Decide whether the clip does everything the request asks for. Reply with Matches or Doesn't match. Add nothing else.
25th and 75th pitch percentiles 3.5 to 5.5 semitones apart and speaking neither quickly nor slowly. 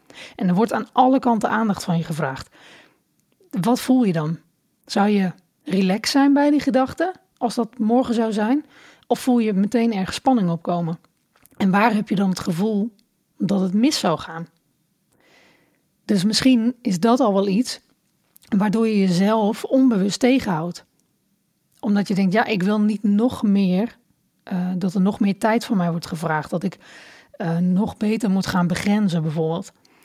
Matches